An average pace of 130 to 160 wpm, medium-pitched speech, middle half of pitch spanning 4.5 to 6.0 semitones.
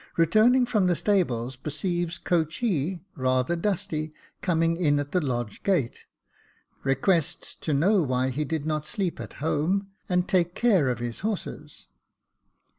Yes: average, 140 wpm; medium, 165 Hz; average, 4.8 semitones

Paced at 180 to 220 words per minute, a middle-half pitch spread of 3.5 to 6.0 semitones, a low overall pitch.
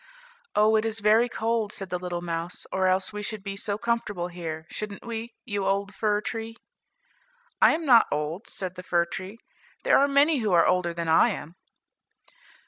No: average, 190 wpm; average, 3.9 semitones; high, 200 Hz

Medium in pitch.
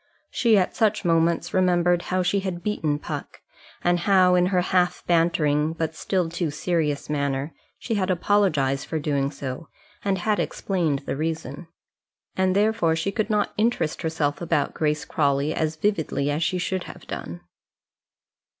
Yes: medium, 170 Hz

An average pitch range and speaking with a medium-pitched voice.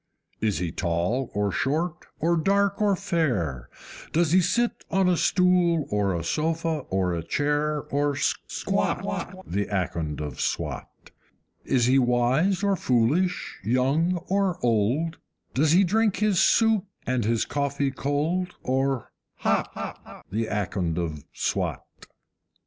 No: wide, 9.0 semitones; medium, 145 Hz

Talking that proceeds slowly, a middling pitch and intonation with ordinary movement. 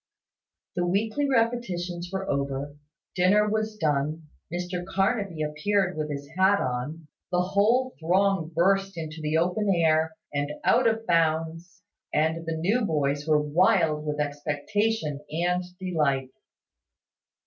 Yes: slow, 125 wpm; medium, 170 Hz; average, 4.4 semitones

